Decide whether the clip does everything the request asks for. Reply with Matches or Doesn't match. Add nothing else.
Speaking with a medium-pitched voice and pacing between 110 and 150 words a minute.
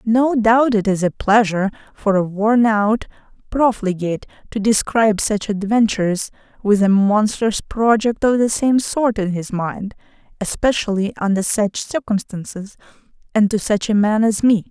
Doesn't match